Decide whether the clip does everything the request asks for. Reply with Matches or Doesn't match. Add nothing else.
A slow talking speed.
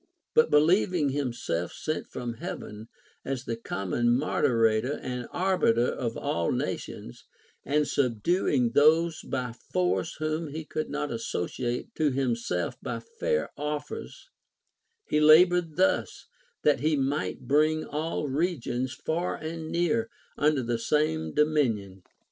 Matches